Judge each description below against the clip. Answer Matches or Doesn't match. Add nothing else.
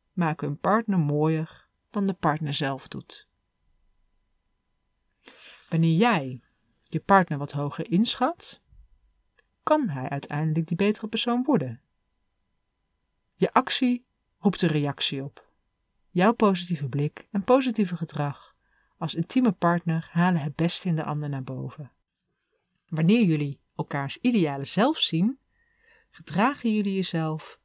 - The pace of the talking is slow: Matches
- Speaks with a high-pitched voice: Doesn't match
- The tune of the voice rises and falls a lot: Matches